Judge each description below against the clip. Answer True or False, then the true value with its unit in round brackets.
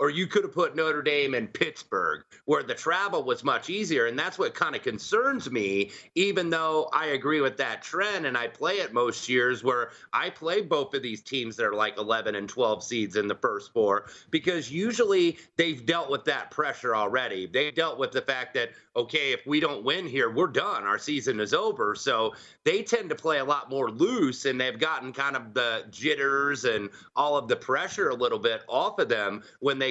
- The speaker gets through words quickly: True (215 wpm)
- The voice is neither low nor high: True (155 Hz)